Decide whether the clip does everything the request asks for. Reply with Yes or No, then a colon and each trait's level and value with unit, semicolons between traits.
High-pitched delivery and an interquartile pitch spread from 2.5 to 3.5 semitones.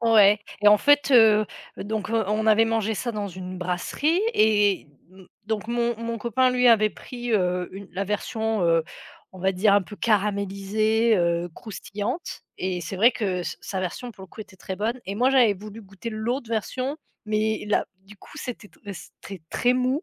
Yes: high, 215 Hz; average, 3.1 semitones